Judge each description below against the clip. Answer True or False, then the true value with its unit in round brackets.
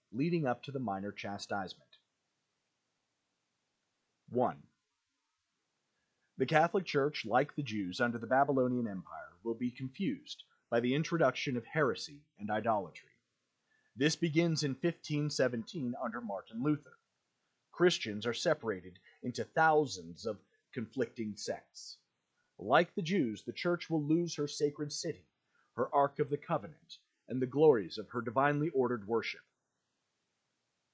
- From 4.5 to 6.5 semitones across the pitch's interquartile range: True (4.9 semitones)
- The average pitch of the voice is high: False (140 Hz)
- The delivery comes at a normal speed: False (125 wpm)